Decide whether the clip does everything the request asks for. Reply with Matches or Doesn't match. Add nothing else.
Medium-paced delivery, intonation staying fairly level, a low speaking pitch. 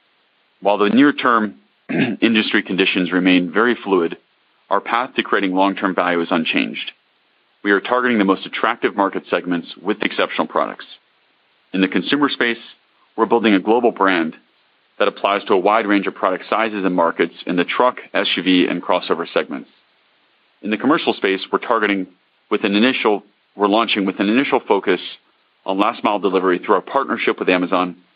Doesn't match